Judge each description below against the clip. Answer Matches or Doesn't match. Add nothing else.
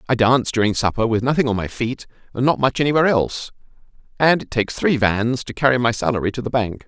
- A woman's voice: Doesn't match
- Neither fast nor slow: Doesn't match